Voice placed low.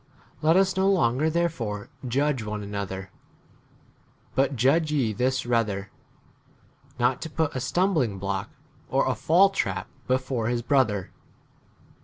Yes: low, 130 Hz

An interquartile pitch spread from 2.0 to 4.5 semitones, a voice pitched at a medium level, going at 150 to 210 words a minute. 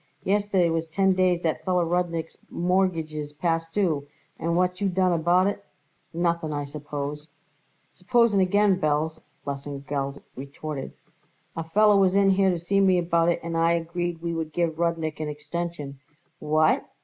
Yes: average, 2.9 semitones; medium, 170 Hz; average, 160 wpm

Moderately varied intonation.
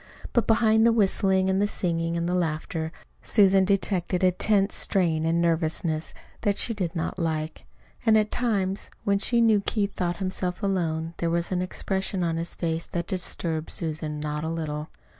Yes: average, 3.3 semitones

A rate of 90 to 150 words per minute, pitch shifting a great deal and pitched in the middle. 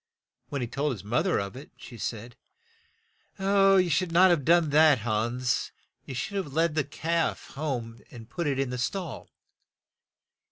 No: average, 170 wpm; wide, 5.7 semitones; medium, 145 Hz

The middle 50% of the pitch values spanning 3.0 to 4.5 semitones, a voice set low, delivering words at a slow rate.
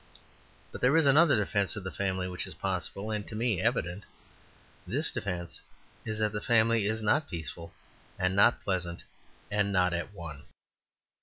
No: average, 3.3 semitones; low, 100 Hz; average, 165 wpm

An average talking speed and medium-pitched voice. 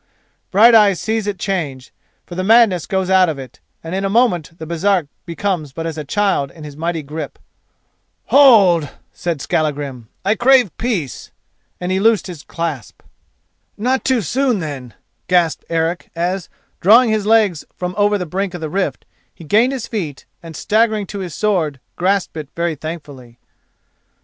Yes: average, 165 wpm; medium, 180 Hz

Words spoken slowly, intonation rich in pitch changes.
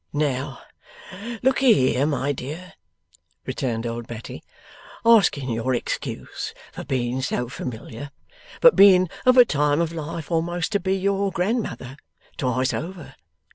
Yes: slow, 130 wpm; wide, 6.3 semitones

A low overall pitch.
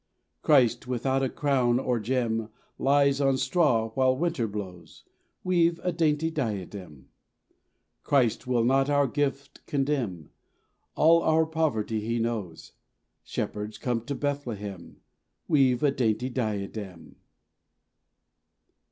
Yes: low, 130 Hz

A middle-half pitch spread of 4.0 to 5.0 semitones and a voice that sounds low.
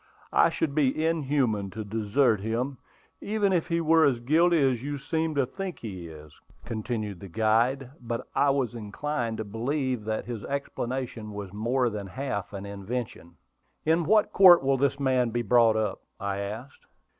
Yes: average, 4.7 semitones; low, 120 Hz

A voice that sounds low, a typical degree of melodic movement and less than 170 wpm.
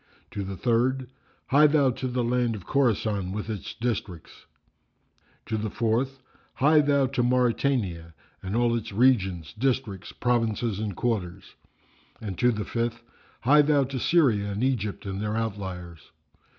Yes: low, 115 Hz; average, 4.2 semitones; average, 150 wpm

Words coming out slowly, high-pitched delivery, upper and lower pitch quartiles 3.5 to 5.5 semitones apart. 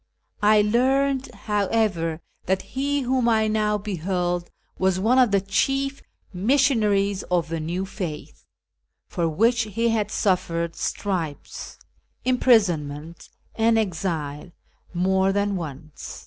Yes: slow, 115 wpm; high, 200 Hz; average, 4.6 semitones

